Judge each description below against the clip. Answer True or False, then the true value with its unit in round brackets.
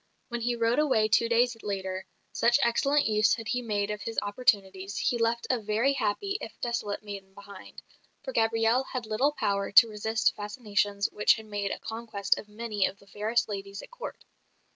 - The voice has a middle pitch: False (220 Hz)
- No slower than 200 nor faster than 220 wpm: False (185 wpm)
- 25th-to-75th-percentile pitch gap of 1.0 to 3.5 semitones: True (2.7 semitones)